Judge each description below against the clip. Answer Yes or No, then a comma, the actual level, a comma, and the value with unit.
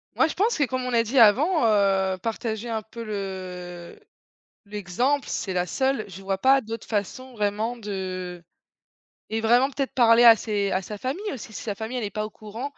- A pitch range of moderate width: Yes, average, 4.2 semitones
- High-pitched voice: Yes, high, 220 Hz